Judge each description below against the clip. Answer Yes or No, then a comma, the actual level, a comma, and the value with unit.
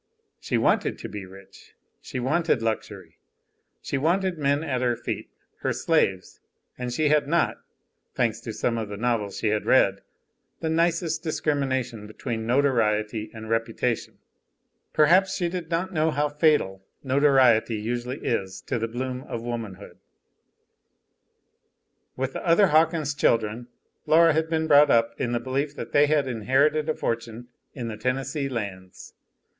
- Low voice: Yes, low, 130 Hz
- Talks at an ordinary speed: Yes, average, 150 wpm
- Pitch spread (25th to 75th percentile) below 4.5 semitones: No, average, 5.0 semitones